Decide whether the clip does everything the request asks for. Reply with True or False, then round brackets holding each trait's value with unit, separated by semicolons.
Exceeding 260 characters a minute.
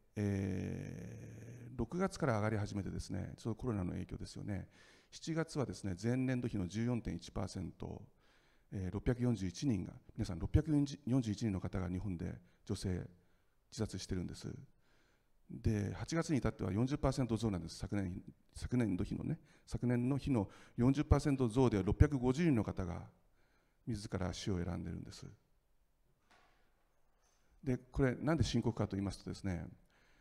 False (235 characters per minute)